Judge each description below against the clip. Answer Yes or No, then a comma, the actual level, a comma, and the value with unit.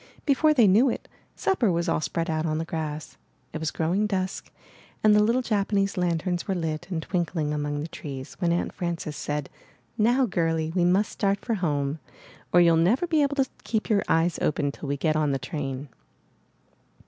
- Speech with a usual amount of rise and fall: Yes, average, 4.8 semitones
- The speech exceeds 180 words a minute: Yes, average, 195 wpm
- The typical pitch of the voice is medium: Yes, medium, 170 Hz